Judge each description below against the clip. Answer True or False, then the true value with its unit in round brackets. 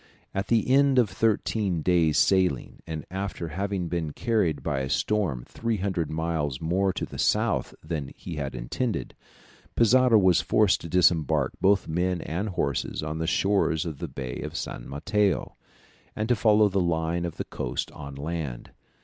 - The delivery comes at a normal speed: True (165 wpm)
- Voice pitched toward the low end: True (85 Hz)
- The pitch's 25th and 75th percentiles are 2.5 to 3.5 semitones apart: False (4.7 semitones)